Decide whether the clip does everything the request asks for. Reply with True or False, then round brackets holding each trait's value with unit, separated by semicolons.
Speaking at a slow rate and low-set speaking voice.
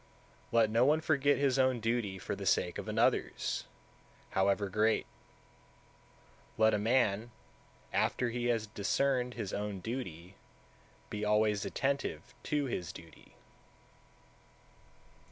True (120 wpm; 110 Hz)